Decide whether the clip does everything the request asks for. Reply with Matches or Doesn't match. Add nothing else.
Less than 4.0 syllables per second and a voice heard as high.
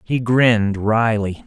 Doesn't match